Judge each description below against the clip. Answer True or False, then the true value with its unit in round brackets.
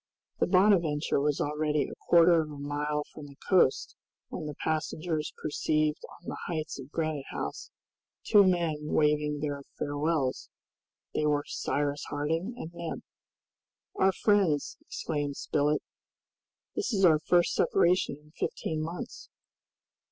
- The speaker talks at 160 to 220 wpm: False (135 wpm)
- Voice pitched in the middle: True (155 Hz)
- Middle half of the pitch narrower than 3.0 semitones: True (2.5 semitones)